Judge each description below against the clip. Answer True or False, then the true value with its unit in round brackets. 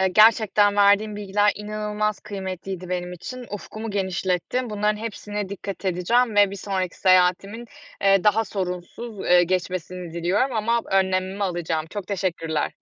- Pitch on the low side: False (195 Hz)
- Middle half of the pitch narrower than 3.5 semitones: True (2.4 semitones)